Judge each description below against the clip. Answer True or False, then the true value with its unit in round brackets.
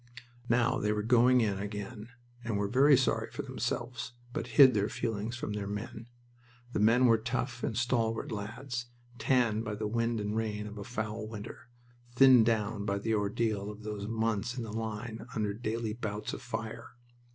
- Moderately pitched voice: False (110 Hz)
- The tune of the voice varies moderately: False (2.2 semitones)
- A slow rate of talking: False (180 wpm)